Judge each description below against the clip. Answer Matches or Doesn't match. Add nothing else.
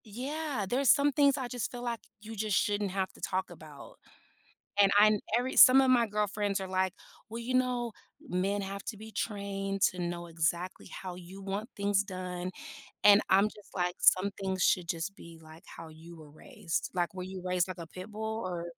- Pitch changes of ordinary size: Matches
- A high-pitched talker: Matches